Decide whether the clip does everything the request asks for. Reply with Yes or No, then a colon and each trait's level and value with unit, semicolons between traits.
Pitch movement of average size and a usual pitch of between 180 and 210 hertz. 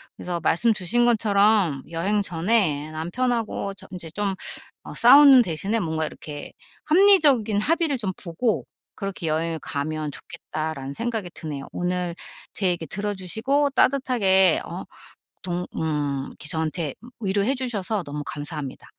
No: wide, 6.1 semitones; high, 190 Hz